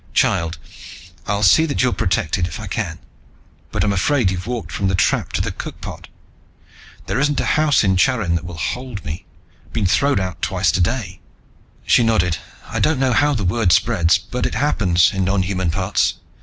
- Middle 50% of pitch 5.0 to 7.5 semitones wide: Yes, wide, 5.6 semitones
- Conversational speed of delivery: Yes, average, 185 wpm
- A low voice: Yes, very low, 95 Hz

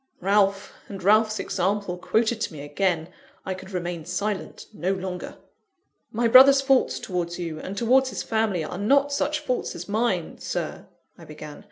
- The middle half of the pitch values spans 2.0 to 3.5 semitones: No, average, 4.3 semitones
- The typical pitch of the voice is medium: No, high, 195 Hz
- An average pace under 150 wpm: No, average, 165 wpm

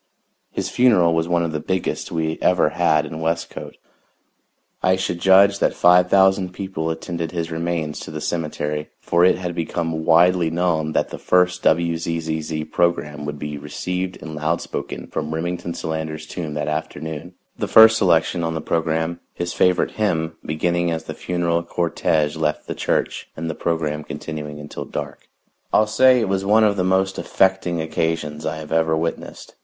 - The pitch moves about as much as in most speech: No, narrow, 2.3 semitones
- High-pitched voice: No, very low, 85 Hz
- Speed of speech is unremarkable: Yes, average, 170 wpm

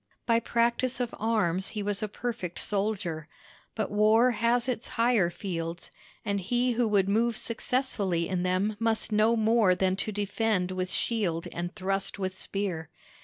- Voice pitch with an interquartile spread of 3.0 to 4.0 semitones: Yes, average, 3.7 semitones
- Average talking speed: Yes, average, 160 wpm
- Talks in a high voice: Yes, high, 210 Hz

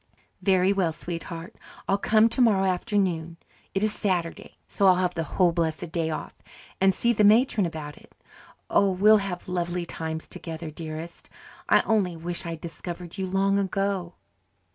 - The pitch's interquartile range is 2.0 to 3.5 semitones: Yes, average, 2.9 semitones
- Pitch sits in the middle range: Yes, medium, 180 Hz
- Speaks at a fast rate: No, average, 160 wpm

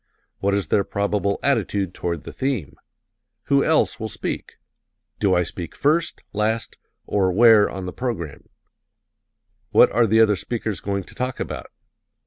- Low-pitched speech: Yes, low, 105 Hz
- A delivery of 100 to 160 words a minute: Yes, average, 150 wpm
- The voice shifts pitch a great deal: No, average, 3.6 semitones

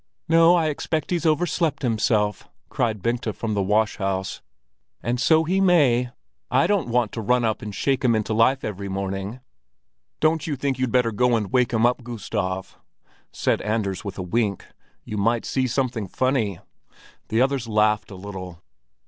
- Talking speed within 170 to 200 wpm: Yes, average, 175 wpm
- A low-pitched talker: Yes, low, 115 Hz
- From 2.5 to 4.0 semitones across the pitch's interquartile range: No, average, 4.4 semitones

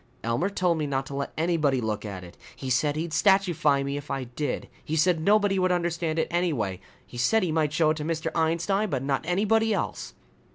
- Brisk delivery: Yes, fast, 215 wpm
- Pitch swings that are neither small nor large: Yes, average, 4.4 semitones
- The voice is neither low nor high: Yes, medium, 160 Hz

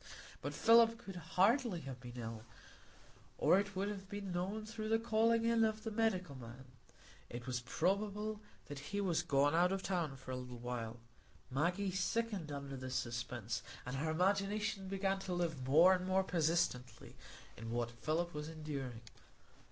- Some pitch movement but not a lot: No, wide, 7.4 semitones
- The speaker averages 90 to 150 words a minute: No, average, 170 wpm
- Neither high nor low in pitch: Yes, medium, 175 Hz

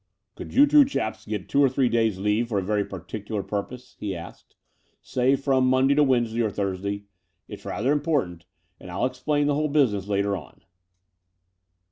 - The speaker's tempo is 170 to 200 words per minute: Yes, average, 175 wpm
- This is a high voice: No, low, 115 Hz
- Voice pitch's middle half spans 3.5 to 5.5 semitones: Yes, average, 5.2 semitones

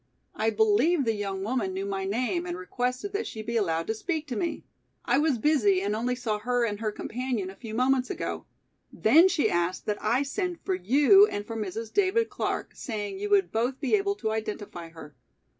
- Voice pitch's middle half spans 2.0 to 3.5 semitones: No, average, 5.2 semitones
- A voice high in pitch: Yes, high, 225 Hz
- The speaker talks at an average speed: No, fast, 210 wpm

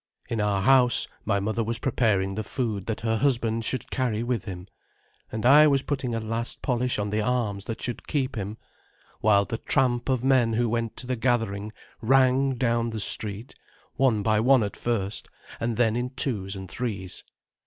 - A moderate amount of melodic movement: Yes, average, 3.0 semitones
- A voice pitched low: Yes, low, 115 Hz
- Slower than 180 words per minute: No, average, 185 wpm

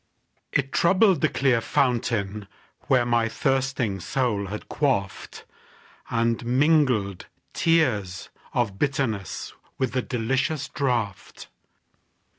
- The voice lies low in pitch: Yes, low, 120 Hz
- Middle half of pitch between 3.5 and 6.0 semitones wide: Yes, average, 4.2 semitones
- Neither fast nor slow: No, slow, 90 wpm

